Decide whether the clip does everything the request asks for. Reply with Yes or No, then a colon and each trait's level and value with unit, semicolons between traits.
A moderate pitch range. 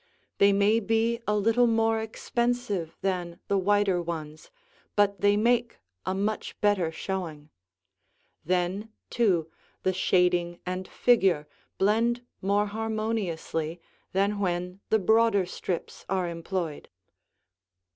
Yes: average, 3.8 semitones